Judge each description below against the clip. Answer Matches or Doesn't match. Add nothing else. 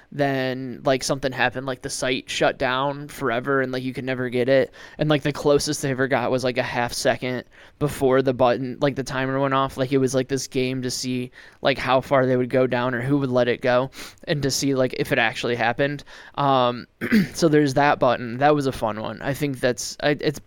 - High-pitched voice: Doesn't match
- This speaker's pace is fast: Matches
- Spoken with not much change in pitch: Matches